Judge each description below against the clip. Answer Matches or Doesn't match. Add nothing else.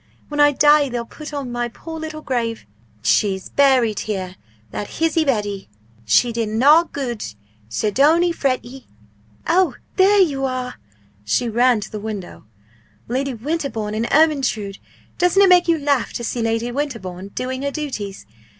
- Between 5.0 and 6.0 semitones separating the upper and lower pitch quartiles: Matches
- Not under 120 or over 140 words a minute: Doesn't match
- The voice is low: Doesn't match